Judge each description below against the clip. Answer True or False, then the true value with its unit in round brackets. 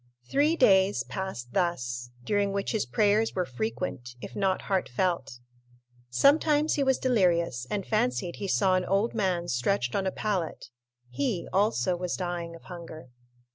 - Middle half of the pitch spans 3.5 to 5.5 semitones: True (4.4 semitones)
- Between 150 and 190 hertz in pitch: True (185 Hz)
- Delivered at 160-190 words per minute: False (150 wpm)